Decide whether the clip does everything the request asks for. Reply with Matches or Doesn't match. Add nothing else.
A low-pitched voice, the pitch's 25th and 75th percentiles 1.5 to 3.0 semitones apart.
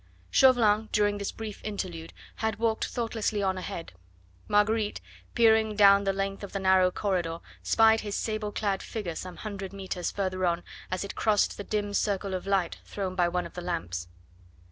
Doesn't match